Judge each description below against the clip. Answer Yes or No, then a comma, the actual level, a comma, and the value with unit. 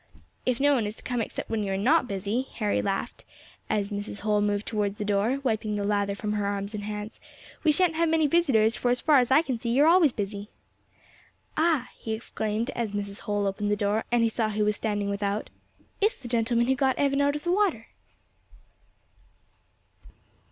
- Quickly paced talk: Yes, fast, 210 wpm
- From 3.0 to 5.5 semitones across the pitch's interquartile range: Yes, average, 4.4 semitones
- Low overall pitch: No, high, 220 Hz